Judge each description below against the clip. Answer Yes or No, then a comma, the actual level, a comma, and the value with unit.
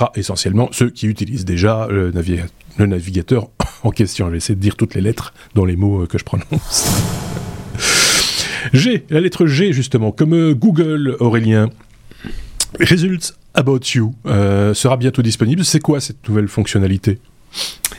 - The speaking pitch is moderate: No, low, 115 Hz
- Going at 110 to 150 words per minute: Yes, slow, 145 wpm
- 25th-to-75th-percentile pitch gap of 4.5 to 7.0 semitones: Yes, average, 4.9 semitones